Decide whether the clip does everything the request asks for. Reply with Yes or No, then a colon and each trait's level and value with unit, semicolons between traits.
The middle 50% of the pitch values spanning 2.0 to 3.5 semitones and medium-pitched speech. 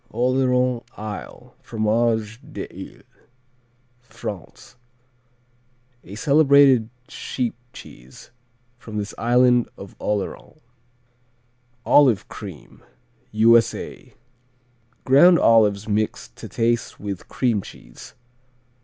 No: average, 3.0 semitones; low, 115 Hz